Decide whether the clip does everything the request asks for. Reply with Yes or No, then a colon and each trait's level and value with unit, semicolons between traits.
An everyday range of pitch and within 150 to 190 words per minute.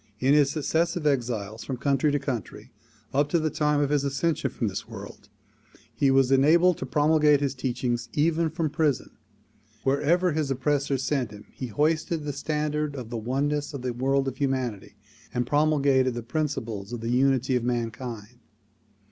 Yes: average, 3.4 semitones; average, 170 wpm